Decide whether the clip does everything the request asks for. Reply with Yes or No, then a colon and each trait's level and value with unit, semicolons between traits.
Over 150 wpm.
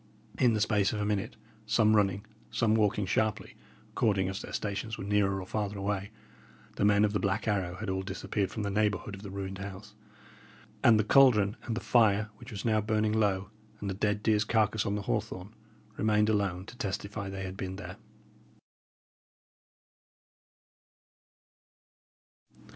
Yes: average, 165 wpm